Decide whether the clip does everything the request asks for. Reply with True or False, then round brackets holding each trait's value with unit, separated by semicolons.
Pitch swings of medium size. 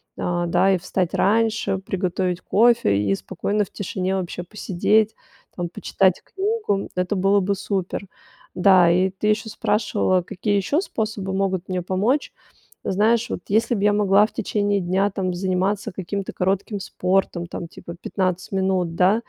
False (2.1 semitones)